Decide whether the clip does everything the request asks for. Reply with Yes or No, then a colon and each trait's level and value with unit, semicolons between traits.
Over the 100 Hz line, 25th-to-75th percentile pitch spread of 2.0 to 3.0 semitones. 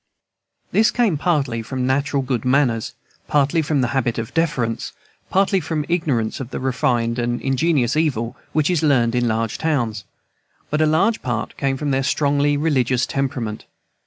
No: low, 135 Hz; average, 4.2 semitones